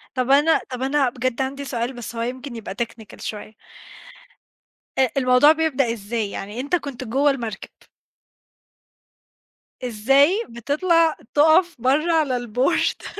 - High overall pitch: Yes, very high, 260 Hz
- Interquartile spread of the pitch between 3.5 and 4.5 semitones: Yes, average, 3.9 semitones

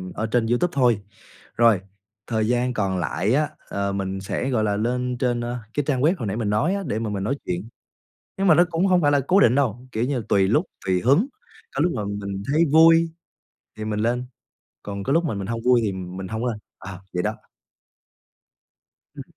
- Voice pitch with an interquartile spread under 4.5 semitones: No, wide, 5.5 semitones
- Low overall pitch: Yes, low, 115 Hz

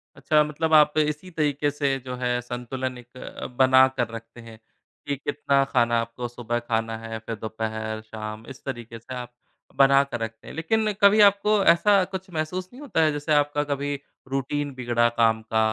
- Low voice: Yes, low, 130 Hz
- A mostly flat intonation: No, average, 4.5 semitones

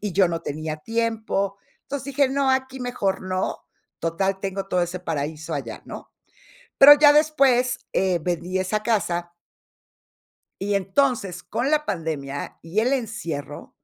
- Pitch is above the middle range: Yes, high, 195 Hz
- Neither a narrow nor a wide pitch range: No, wide, 6.4 semitones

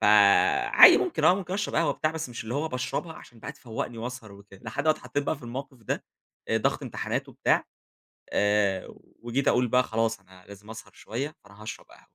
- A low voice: Yes, low, 120 Hz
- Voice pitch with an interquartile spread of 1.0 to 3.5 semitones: No, average, 4.9 semitones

